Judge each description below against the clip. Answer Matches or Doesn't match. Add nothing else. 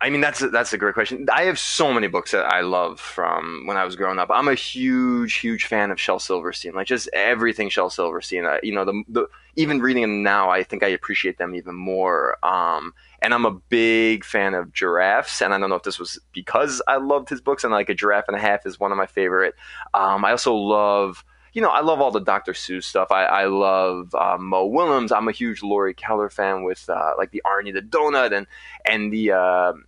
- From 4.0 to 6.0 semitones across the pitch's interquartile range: Doesn't match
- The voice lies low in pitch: Matches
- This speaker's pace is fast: Matches